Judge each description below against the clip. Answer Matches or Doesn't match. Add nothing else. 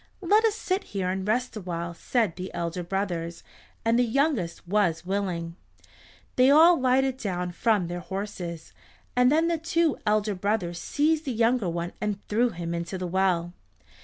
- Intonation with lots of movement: Matches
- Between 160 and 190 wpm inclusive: Matches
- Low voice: Doesn't match